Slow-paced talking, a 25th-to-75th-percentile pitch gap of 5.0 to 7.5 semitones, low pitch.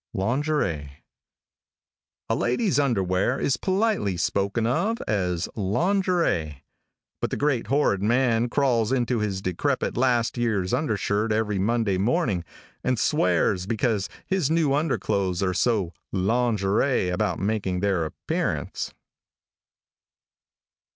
Yes: slow, 110 wpm; wide, 5.6 semitones; low, 110 Hz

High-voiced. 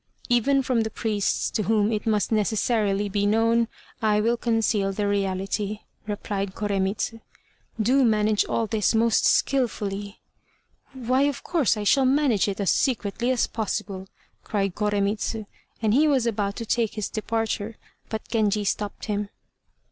Yes: high, 215 Hz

